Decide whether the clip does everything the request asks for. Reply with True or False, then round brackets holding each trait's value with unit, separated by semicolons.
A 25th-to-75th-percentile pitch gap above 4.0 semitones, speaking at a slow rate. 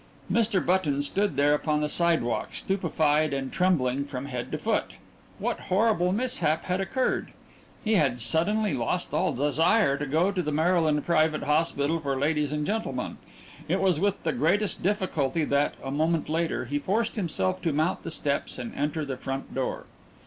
False (4.5 semitones; 170 wpm)